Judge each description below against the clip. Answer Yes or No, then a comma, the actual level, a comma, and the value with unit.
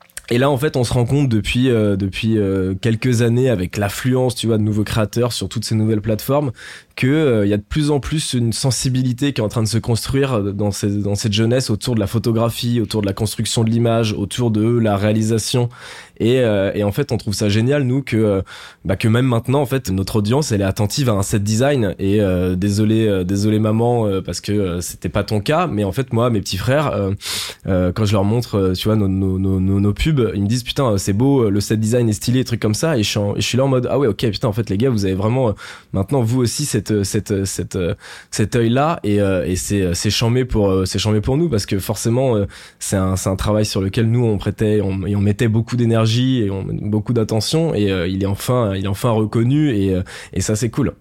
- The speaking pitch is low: Yes, low, 110 Hz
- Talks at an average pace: No, fast, 250 wpm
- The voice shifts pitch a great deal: No, average, 3.4 semitones